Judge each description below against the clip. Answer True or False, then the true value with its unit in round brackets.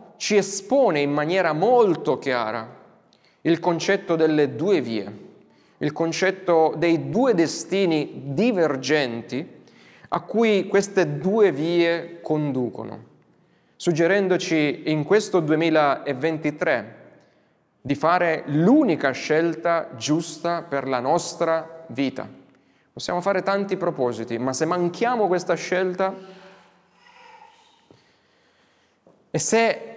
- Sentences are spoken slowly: True (95 wpm)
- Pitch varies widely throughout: False (3.9 semitones)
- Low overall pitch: False (170 Hz)